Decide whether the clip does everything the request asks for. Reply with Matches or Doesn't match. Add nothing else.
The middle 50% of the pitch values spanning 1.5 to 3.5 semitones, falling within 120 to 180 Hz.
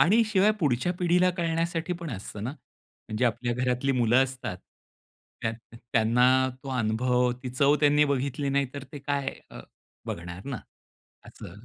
Doesn't match